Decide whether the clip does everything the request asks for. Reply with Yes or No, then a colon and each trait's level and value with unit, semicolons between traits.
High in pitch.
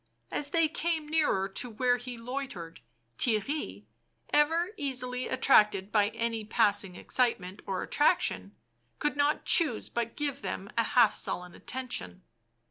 Yes: high, 245 Hz